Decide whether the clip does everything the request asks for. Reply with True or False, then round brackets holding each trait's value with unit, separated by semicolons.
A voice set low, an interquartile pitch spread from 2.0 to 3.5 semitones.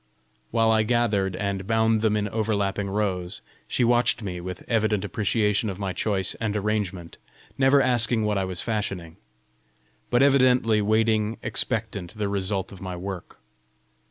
True (105 Hz; 2.6 semitones)